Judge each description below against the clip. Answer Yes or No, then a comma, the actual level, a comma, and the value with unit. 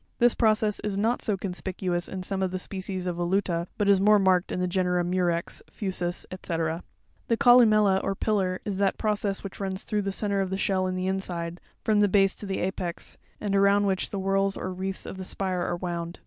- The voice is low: No, high, 190 Hz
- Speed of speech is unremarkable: No, fast, 220 wpm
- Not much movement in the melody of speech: Yes, narrow, 1.7 semitones